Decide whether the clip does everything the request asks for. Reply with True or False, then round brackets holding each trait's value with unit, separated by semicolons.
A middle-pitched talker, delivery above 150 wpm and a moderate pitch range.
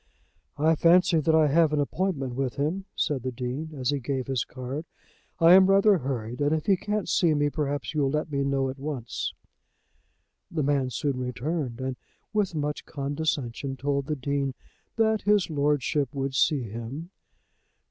True (145 Hz; 170 wpm; 3.1 semitones)